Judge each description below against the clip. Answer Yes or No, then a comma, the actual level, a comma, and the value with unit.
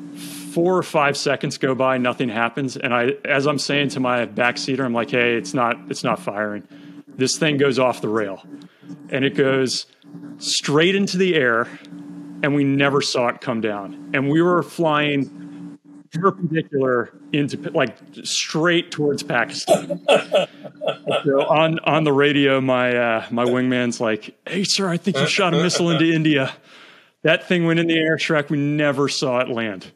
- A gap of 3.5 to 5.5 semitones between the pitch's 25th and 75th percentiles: Yes, average, 3.9 semitones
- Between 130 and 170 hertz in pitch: Yes, medium, 140 Hz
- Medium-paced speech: Yes, average, 170 wpm